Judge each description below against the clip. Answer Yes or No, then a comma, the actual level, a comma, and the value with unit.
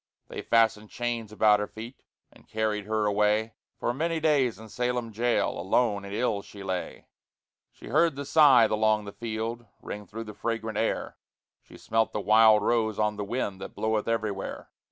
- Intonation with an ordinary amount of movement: No, narrow, 2.1 semitones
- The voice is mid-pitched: No, low, 110 Hz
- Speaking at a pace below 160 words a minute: No, average, 175 wpm